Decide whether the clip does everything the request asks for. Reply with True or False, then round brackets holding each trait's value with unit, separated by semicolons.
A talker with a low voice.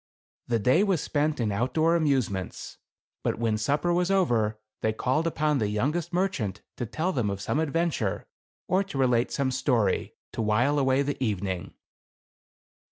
True (130 Hz)